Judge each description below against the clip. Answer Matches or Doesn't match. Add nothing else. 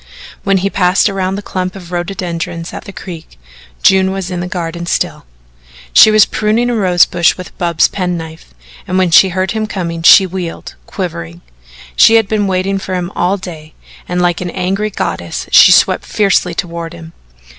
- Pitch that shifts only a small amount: Matches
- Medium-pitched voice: Matches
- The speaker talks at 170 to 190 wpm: Matches